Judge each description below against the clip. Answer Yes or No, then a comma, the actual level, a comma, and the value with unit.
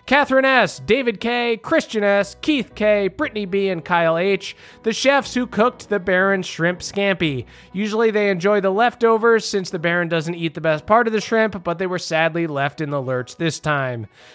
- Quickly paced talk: No, average, 195 wpm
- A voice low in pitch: No, high, 200 Hz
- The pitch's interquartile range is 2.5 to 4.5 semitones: No, average, 5.2 semitones